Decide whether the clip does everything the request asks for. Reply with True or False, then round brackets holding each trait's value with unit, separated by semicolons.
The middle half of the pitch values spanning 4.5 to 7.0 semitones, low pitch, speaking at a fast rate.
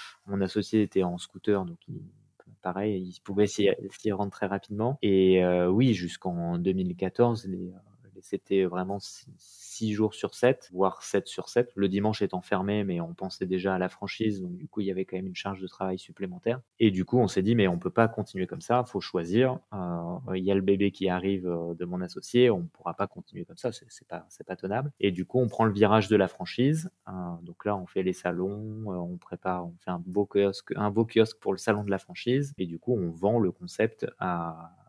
False (3.0 semitones; 100 Hz; 235 wpm)